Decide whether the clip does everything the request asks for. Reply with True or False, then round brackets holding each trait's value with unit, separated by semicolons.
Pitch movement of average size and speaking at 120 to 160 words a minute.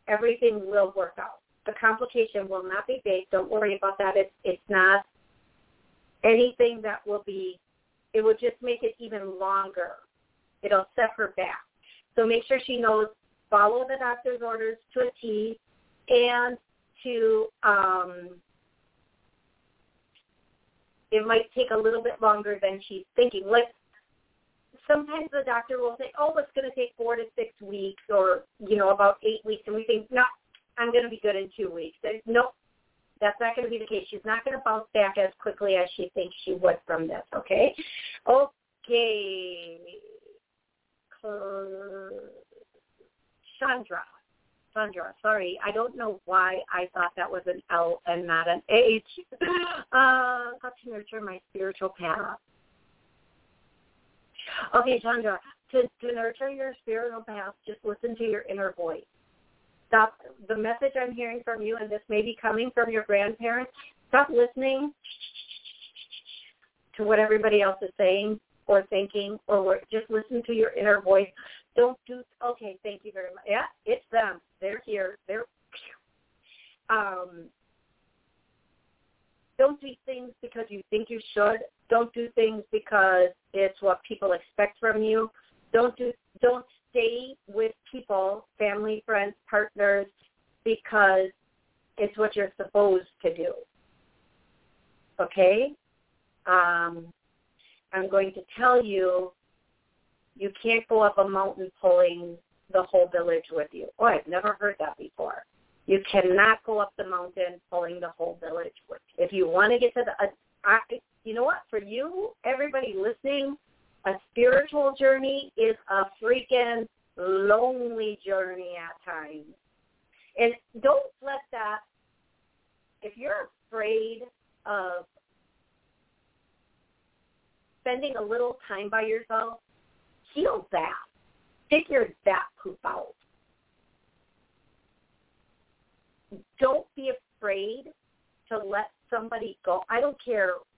True (4.0 semitones; 140 wpm)